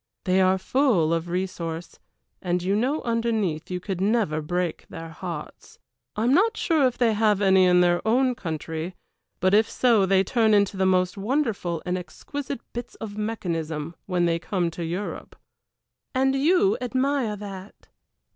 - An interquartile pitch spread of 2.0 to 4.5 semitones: No, average, 4.9 semitones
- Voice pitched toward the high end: Yes, high, 195 Hz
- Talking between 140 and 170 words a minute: Yes, average, 165 wpm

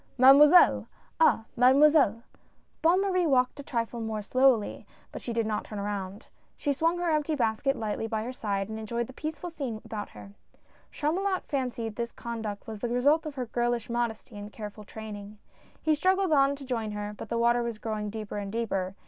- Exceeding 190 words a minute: Yes, average, 200 wpm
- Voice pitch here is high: Yes, high, 235 Hz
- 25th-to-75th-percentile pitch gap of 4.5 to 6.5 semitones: Yes, average, 4.8 semitones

